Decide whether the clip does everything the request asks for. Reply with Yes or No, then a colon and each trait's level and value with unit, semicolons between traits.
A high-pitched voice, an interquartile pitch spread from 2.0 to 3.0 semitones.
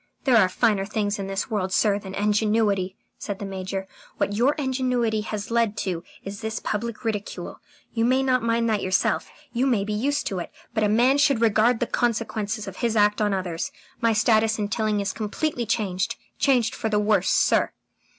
Yes: high, 215 Hz; narrow, 2.5 semitones